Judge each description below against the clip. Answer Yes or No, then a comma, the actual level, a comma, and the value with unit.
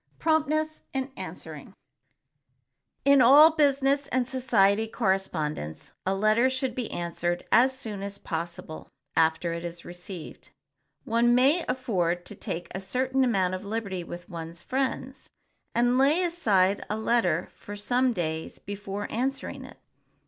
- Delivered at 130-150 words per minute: Yes, average, 140 wpm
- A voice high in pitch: Yes, high, 220 Hz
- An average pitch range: No, wide, 6.7 semitones